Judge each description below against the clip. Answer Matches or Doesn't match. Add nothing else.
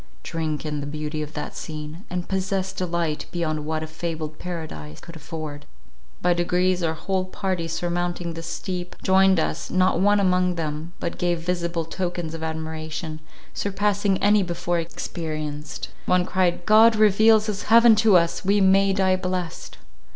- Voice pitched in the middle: Matches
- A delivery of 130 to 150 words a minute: Doesn't match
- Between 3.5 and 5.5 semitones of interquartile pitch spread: Doesn't match